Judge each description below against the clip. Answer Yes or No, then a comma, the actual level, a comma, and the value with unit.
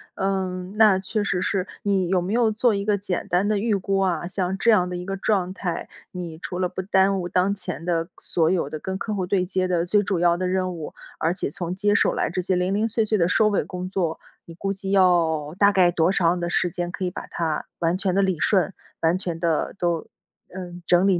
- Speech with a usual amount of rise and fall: No, narrow, 2.0 semitones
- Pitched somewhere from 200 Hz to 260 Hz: No, medium, 185 Hz